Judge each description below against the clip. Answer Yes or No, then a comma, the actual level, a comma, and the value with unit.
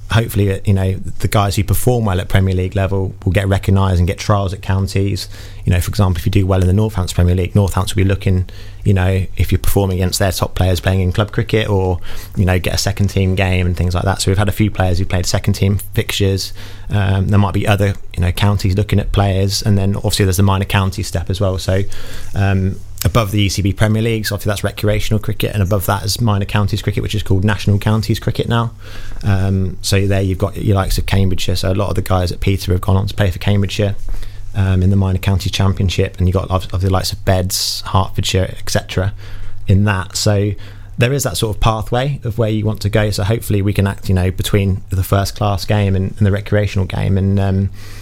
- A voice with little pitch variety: Yes, narrow, 1.5 semitones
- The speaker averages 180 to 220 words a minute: No, fast, 240 wpm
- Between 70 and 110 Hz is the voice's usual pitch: Yes, low, 100 Hz